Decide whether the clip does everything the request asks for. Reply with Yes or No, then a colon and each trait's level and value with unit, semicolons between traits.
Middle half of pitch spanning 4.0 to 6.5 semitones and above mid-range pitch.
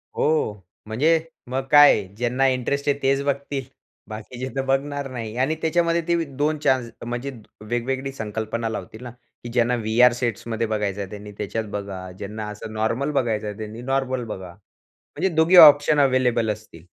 No: average, 4.3 semitones; low, 125 Hz